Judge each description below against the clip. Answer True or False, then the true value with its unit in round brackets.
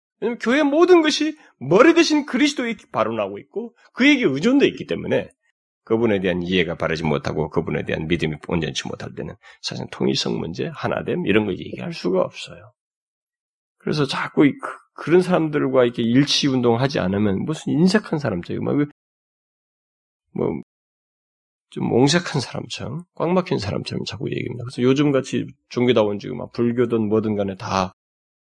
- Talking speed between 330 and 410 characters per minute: True (340 characters per minute)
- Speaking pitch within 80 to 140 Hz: True (135 Hz)